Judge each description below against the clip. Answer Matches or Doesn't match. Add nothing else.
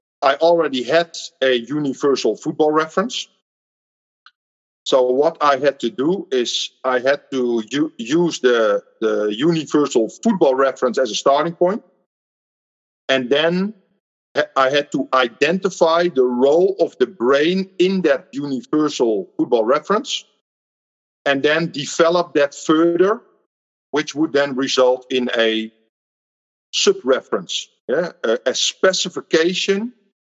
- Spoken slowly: Matches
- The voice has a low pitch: Doesn't match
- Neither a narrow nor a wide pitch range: Doesn't match